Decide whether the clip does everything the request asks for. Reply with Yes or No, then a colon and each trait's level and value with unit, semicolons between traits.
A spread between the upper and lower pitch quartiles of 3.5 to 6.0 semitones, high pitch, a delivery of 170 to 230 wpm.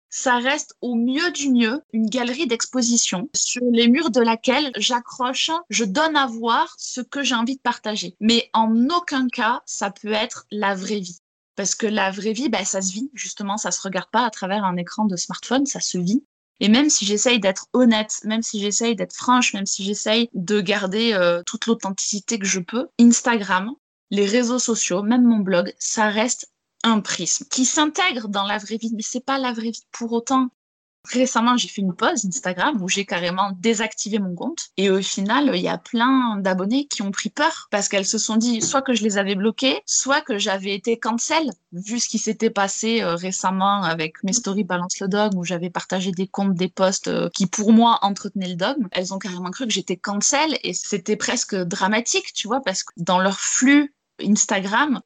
Yes: average, 4.0 semitones; high, 220 Hz; average, 205 wpm